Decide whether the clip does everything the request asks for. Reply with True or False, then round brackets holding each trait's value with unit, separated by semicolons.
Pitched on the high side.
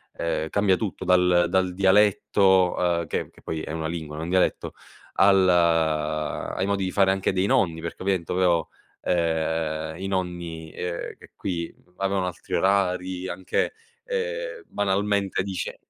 False (90 Hz)